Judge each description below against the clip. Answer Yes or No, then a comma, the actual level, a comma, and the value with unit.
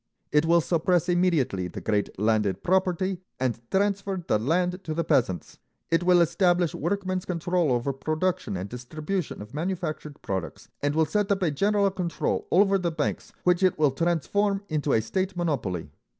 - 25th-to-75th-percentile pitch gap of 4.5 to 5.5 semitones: Yes, average, 5.2 semitones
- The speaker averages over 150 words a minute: Yes, average, 165 wpm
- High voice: No, medium, 170 Hz